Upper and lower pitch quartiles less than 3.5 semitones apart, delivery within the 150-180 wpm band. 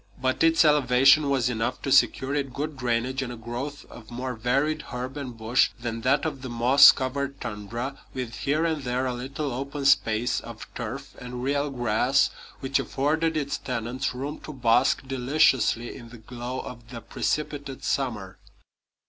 Yes: narrow, 2.5 semitones; average, 170 wpm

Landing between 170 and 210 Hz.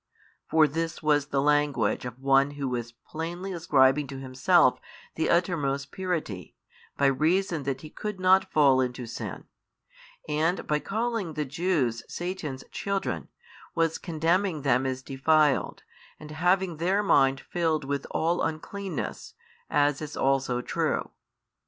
No: medium, 150 Hz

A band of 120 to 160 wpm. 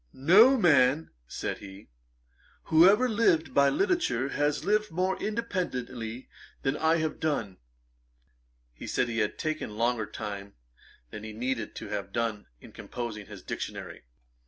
Yes: average, 140 wpm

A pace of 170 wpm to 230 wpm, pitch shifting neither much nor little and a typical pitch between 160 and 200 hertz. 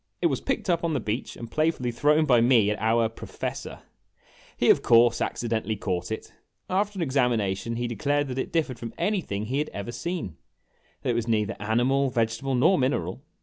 No: average, 195 wpm; average, 4.5 semitones; low, 120 Hz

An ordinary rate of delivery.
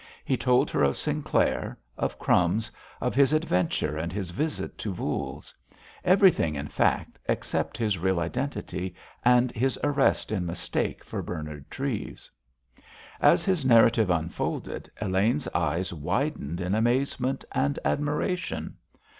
No: slow, 130 wpm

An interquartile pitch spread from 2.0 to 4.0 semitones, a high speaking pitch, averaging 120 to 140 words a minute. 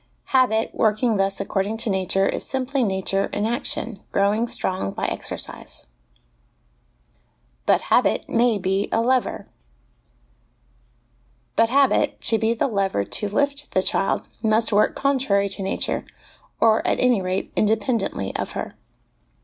Yes: average, 3.5 semitones; high, 215 Hz; slow, 135 wpm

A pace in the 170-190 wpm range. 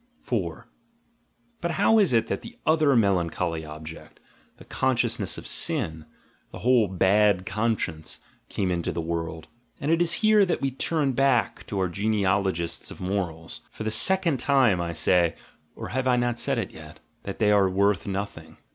Yes: average, 175 wpm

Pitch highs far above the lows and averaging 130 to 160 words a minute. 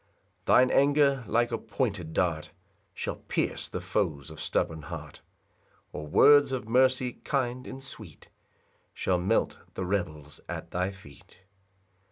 Yes: wide, 7.8 semitones; average, 140 wpm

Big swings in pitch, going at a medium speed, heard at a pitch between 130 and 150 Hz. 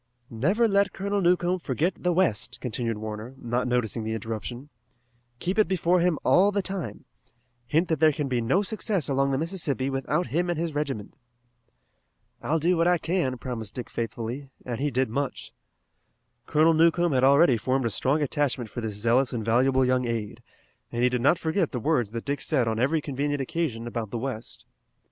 Yes: wide, 5.8 semitones; average, 190 wpm; low, 135 Hz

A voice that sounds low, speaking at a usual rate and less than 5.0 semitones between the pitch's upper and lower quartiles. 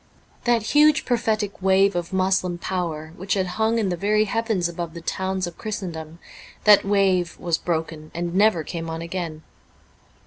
No: medium, 185 Hz; average, 165 wpm; average, 3.5 semitones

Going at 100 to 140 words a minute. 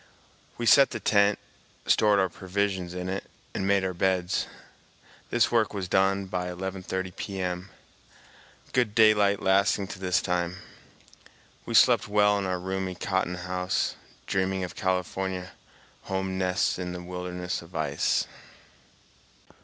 Yes: slow, 135 wpm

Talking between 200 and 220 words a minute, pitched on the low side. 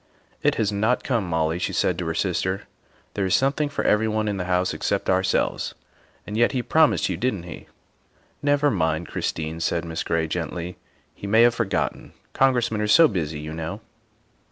Yes: fast, 205 wpm; low, 100 Hz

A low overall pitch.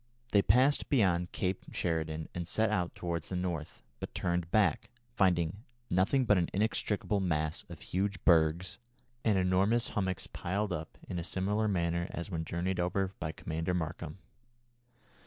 Yes: very low, 90 Hz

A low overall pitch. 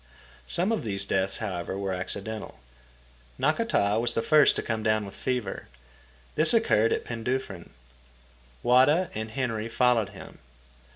Yes: low, 110 Hz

